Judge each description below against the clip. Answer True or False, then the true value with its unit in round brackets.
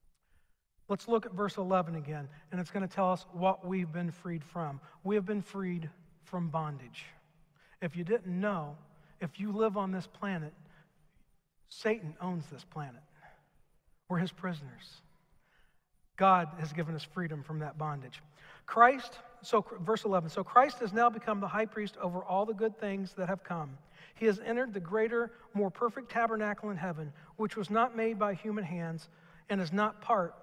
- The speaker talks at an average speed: True (175 wpm)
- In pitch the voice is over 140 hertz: True (185 Hz)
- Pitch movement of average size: True (4.7 semitones)